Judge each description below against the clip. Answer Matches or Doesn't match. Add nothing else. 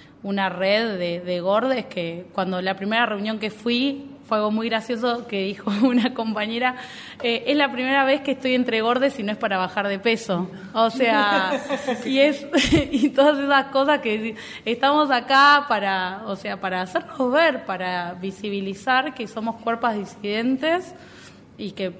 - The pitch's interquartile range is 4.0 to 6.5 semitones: Matches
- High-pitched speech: Matches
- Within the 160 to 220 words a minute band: Matches